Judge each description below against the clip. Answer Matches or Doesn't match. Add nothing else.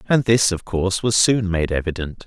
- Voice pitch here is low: Matches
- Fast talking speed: Matches